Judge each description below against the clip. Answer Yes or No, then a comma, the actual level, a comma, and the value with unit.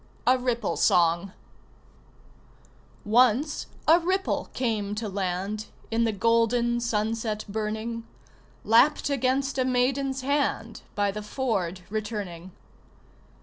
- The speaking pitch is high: Yes, high, 230 Hz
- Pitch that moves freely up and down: No, average, 3.4 semitones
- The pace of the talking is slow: Yes, slow, 105 wpm